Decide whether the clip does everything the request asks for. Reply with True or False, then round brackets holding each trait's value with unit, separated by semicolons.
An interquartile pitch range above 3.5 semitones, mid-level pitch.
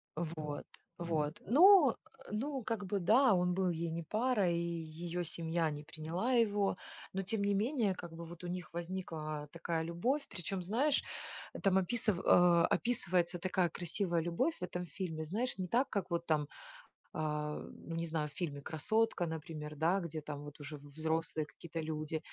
True (3.9 semitones; 175 Hz)